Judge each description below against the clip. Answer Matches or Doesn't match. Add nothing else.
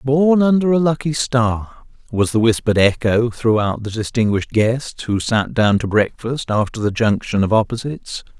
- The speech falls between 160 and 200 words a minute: Matches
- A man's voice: Matches